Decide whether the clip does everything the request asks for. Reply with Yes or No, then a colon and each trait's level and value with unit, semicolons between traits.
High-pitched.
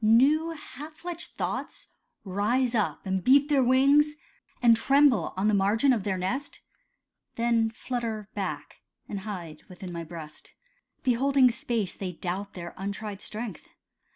Yes: high, 225 Hz